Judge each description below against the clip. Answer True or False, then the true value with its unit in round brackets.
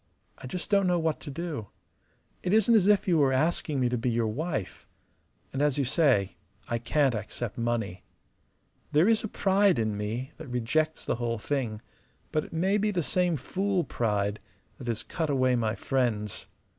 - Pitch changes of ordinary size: False (6.9 semitones)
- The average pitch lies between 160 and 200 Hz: False (135 Hz)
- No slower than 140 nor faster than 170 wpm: False (185 wpm)